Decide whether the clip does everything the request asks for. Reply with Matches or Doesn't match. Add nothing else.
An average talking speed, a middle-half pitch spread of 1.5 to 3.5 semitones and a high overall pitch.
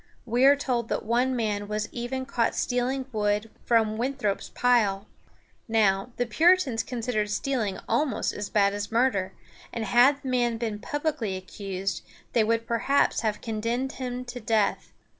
Matches